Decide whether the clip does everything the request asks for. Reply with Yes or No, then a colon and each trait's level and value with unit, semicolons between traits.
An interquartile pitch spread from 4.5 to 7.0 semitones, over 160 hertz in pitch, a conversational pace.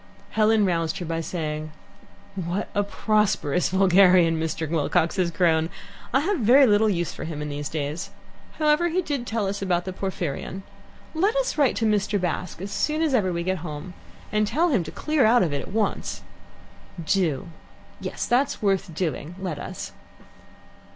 Yes: average, 5.1 semitones; high, 190 Hz; average, 175 wpm